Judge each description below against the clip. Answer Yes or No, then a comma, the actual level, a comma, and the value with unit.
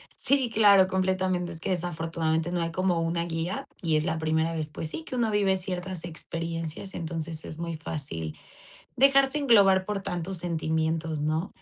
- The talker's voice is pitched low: No, medium, 170 Hz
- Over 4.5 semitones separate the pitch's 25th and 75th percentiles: No, average, 2.8 semitones